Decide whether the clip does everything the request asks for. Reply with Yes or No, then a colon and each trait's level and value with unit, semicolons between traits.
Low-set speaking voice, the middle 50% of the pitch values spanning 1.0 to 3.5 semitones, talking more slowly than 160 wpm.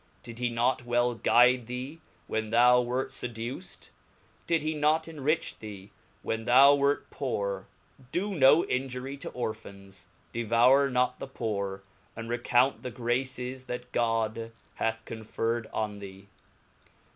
Yes: low, 120 Hz; average, 2.8 semitones; average, 145 wpm